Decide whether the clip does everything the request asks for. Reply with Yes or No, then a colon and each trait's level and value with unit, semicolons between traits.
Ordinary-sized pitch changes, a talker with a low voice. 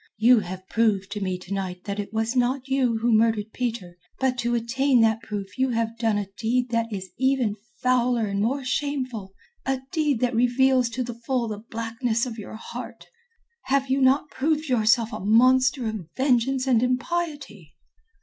No: average, 3.1 semitones; high, 235 Hz